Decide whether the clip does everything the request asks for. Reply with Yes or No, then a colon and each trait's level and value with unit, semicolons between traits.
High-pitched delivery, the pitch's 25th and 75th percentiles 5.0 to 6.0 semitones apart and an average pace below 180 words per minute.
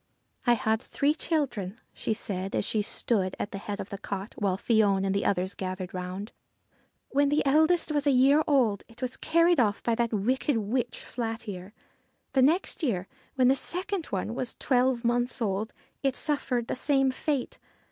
No: high, 235 Hz; wide, 5.4 semitones; average, 190 wpm